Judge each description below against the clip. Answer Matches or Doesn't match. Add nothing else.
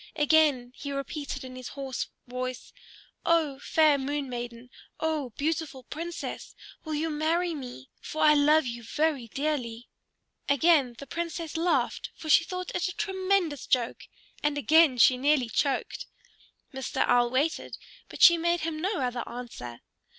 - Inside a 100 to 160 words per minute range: Matches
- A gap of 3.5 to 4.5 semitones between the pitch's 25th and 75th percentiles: Matches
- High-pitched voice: Matches